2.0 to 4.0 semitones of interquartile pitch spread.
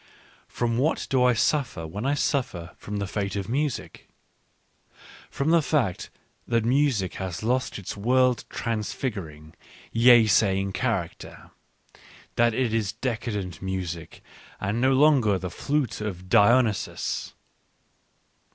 No: average, 4.8 semitones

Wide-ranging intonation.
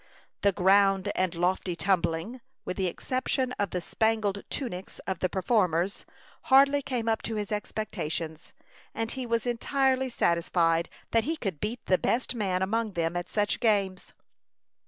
No: average, 4.3 semitones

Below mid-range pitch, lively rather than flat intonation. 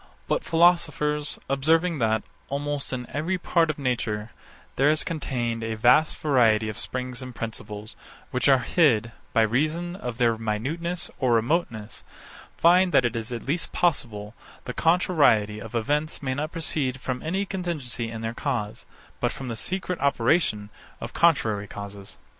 Yes: low, 130 Hz; wide, 5.7 semitones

